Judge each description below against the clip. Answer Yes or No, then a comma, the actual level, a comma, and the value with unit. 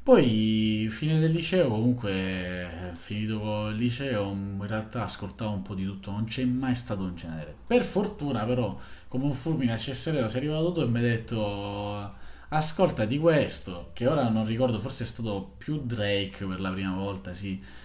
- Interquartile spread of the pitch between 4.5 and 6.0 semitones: Yes, average, 4.9 semitones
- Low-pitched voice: Yes, low, 110 Hz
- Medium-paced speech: No, fast, 180 wpm